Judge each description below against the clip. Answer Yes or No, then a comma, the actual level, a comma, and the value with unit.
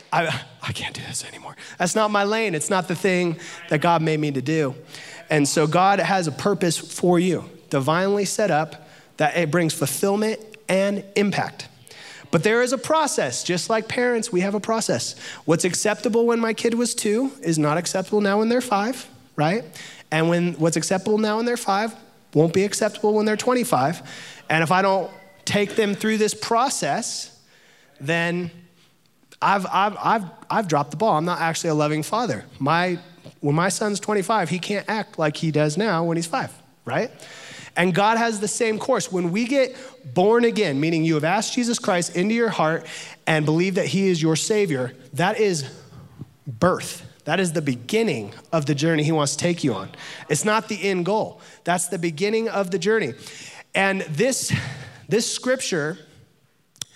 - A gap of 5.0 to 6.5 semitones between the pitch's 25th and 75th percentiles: Yes, average, 5.3 semitones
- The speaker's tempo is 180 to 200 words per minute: Yes, average, 185 wpm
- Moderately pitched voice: Yes, medium, 180 Hz